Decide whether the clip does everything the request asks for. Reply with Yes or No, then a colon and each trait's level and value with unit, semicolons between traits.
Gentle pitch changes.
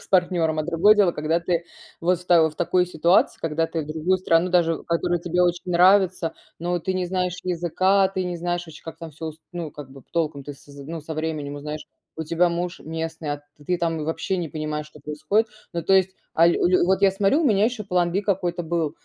Yes: narrow, 2.3 semitones